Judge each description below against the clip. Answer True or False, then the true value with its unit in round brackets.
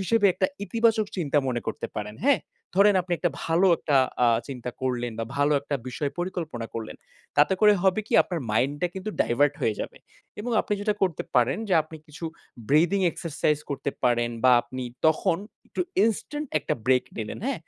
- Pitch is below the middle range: False (155 Hz)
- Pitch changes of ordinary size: False (6.9 semitones)